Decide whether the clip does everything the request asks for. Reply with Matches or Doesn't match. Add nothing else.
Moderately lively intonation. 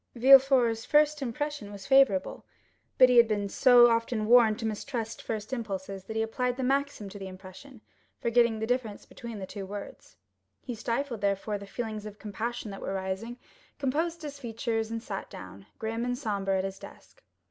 Matches